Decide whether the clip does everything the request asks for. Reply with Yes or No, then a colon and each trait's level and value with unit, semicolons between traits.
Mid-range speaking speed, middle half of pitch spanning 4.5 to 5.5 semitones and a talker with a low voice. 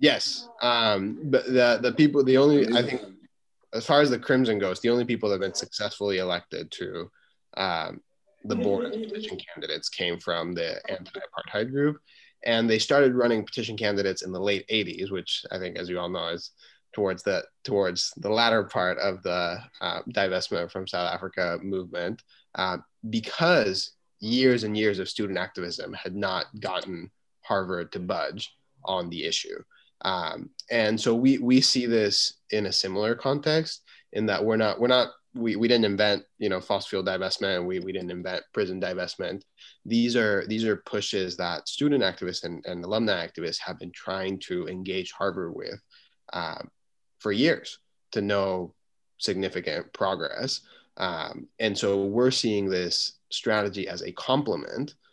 Yes: average, 170 wpm; average, 4.9 semitones; low, 110 Hz